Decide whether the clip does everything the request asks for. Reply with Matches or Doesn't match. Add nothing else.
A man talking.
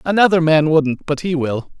Matches